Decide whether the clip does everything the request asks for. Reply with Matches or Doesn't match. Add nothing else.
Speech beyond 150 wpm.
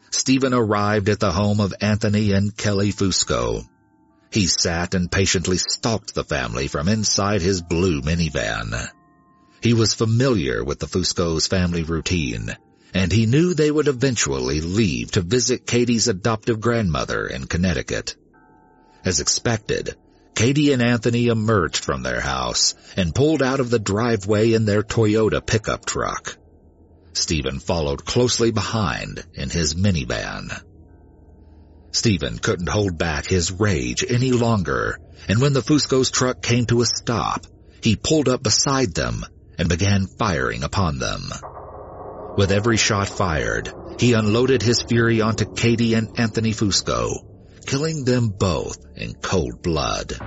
Doesn't match